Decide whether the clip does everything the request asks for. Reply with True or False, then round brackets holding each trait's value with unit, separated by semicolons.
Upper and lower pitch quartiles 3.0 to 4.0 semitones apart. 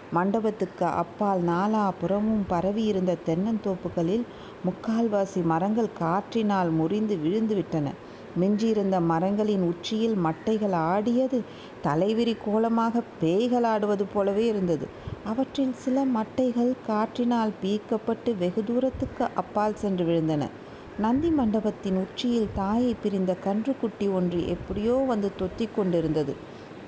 True (3.7 semitones)